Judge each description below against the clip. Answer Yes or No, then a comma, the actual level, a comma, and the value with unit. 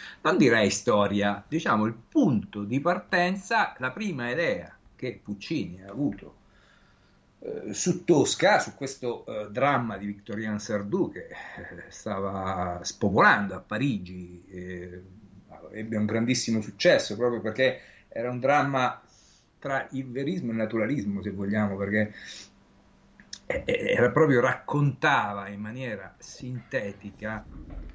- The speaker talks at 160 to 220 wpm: No, average, 120 wpm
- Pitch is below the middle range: Yes, low, 110 Hz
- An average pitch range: Yes, average, 4.3 semitones